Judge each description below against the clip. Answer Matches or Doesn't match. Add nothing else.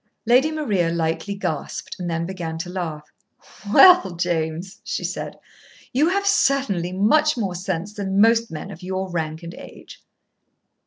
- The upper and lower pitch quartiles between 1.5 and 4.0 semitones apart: Doesn't match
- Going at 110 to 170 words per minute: Matches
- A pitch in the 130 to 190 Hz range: Matches